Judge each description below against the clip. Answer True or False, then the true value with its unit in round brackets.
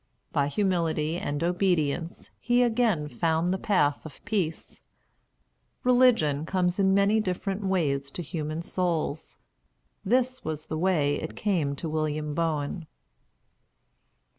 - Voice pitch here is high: False (170 Hz)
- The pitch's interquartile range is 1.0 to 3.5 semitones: False (4.1 semitones)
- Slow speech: True (120 wpm)